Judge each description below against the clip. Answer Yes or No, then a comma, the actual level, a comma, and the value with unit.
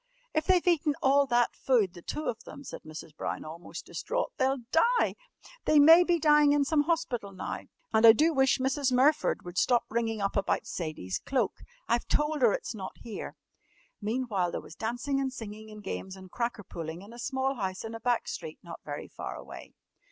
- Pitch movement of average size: No, wide, 6.2 semitones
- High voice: Yes, high, 240 Hz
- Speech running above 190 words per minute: Yes, average, 200 wpm